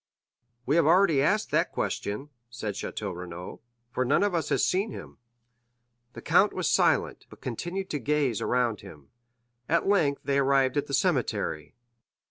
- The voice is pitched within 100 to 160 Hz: Yes, medium, 140 Hz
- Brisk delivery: No, average, 160 wpm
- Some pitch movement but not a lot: No, wide, 6.6 semitones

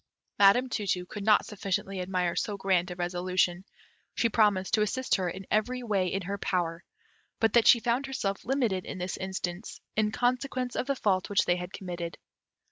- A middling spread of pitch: Yes, average, 3.6 semitones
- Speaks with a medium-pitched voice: No, high, 195 Hz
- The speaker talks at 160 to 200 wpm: Yes, average, 190 wpm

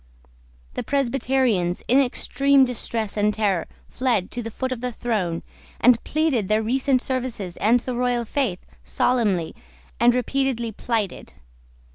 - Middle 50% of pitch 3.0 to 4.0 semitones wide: Yes, average, 3.5 semitones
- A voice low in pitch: No, high, 240 Hz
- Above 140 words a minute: No, slow, 135 wpm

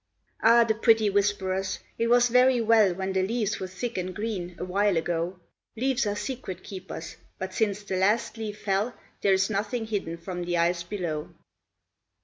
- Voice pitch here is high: Yes, high, 200 Hz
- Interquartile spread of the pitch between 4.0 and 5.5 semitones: No, average, 3.3 semitones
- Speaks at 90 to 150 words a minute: No, average, 170 wpm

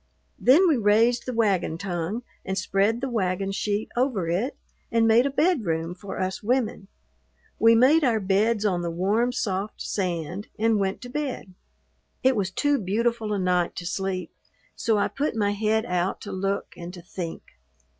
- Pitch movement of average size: Yes, average, 4.0 semitones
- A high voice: Yes, high, 205 Hz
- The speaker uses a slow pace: No, average, 175 wpm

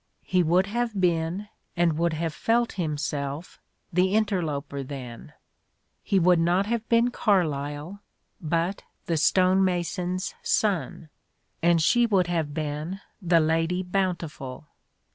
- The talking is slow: Yes, slow, 125 wpm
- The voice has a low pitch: No, medium, 175 Hz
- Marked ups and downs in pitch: No, average, 3.4 semitones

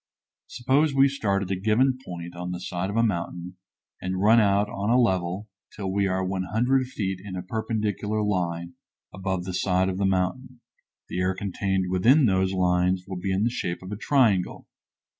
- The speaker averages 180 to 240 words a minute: Yes, average, 190 wpm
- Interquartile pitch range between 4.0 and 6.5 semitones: No, average, 3.0 semitones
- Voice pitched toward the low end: Yes, very low, 95 Hz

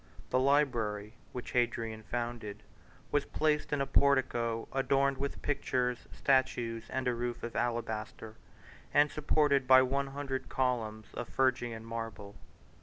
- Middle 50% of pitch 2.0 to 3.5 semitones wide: Yes, average, 3.1 semitones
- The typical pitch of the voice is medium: No, low, 125 Hz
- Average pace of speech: No, slow, 130 wpm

